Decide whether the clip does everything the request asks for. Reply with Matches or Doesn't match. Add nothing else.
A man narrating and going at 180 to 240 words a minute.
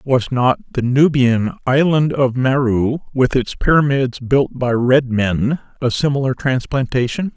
Doesn't match